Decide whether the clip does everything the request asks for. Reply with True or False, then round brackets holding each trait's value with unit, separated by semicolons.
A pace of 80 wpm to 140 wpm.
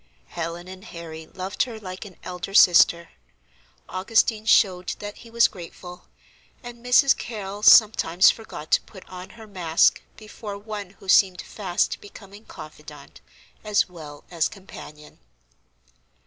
True (135 wpm)